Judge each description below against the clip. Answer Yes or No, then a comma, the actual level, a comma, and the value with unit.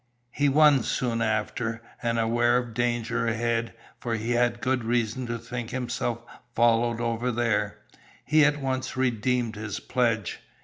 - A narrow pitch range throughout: Yes, narrow, 1.4 semitones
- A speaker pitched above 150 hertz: No, low, 120 Hz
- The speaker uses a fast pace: No, average, 145 wpm